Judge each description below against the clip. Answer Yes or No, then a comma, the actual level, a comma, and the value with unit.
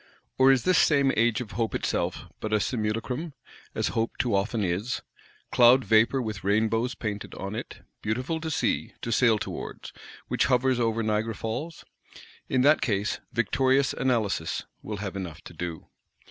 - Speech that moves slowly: No, average, 160 wpm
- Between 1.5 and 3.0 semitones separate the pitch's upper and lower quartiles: No, average, 3.4 semitones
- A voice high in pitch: No, low, 115 Hz